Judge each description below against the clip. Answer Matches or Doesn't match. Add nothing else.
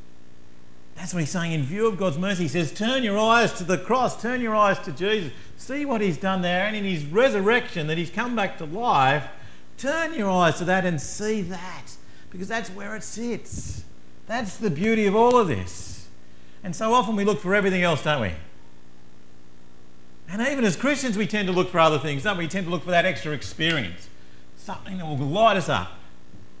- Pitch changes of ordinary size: Doesn't match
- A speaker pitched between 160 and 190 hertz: Matches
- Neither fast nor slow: Doesn't match